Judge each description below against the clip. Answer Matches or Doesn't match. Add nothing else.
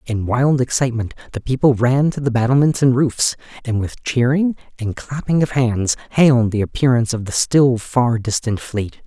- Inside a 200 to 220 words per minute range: Doesn't match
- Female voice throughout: Doesn't match